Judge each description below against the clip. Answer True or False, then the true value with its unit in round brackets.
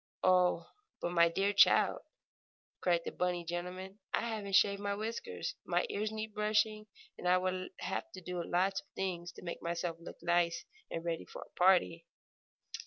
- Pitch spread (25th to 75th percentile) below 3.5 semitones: True (2.8 semitones)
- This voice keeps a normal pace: True (175 wpm)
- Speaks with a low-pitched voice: False (185 Hz)